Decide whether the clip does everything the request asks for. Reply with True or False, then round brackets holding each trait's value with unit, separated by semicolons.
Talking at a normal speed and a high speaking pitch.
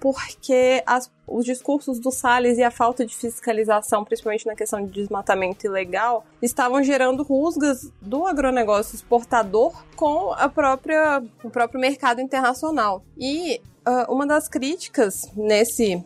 True (135 wpm; 245 Hz)